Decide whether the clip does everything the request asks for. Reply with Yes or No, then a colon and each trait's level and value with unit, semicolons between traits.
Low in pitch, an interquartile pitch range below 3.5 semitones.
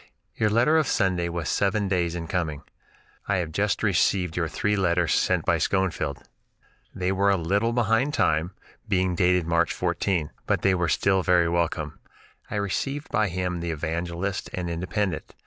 Yes: very low, 90 Hz; average, 2.8 semitones